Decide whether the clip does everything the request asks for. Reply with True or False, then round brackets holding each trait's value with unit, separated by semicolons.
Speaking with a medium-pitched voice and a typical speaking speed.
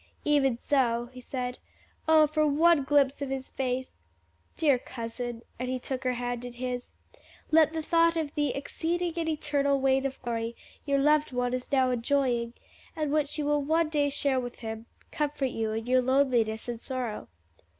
False (265 Hz; 180 wpm)